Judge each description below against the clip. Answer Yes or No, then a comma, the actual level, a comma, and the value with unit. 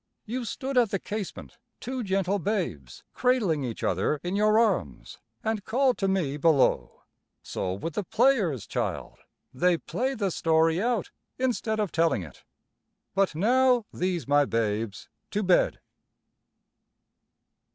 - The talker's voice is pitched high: Yes, high, 195 Hz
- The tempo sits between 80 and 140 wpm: Yes, slow, 135 wpm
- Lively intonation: Yes, wide, 6.7 semitones